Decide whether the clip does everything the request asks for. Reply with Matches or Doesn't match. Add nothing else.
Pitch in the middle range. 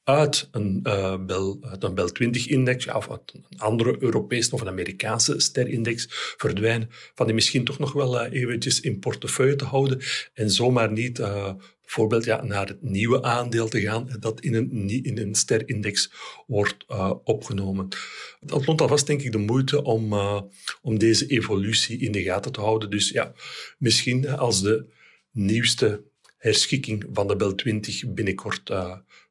Doesn't match